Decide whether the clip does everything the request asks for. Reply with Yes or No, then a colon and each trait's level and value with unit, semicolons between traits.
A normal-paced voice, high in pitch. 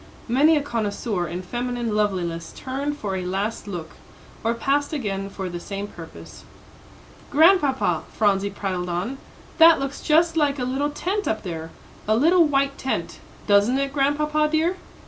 Yes: average, 155 wpm; high, 245 Hz